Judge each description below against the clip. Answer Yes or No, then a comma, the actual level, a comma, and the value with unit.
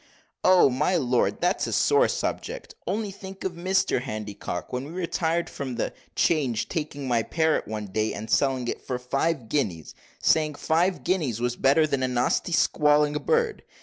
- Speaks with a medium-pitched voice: Yes, medium, 145 Hz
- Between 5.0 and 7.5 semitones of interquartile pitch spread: Yes, wide, 5.5 semitones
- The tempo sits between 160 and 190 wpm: Yes, average, 170 wpm